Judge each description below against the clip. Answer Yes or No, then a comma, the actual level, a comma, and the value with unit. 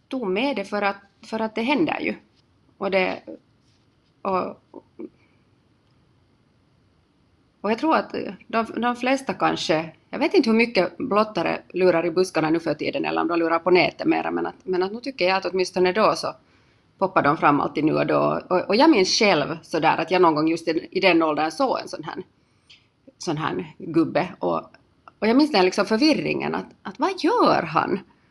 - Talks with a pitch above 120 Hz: Yes, high, 190 Hz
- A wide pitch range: Yes, wide, 6.5 semitones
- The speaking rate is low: No, fast, 195 wpm